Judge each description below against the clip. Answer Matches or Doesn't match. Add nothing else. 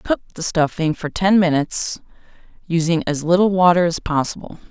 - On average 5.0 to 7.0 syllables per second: Matches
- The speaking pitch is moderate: Matches